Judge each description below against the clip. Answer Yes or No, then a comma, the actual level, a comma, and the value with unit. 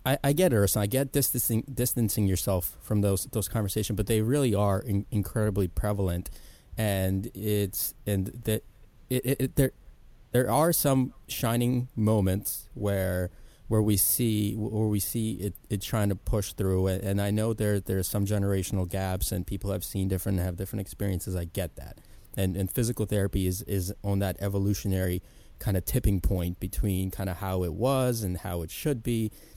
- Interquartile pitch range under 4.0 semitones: Yes, average, 2.8 semitones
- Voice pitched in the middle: No, low, 100 Hz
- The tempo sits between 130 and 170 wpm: No, average, 180 wpm